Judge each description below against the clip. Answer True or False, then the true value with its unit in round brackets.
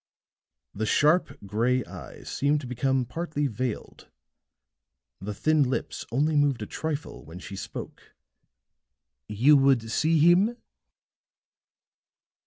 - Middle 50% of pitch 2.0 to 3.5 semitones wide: False (5.0 semitones)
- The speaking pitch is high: False (135 Hz)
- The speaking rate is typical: False (110 wpm)